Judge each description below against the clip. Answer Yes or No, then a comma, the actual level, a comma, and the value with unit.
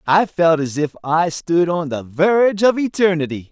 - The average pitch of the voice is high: No, medium, 170 Hz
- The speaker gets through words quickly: No, average, 190 wpm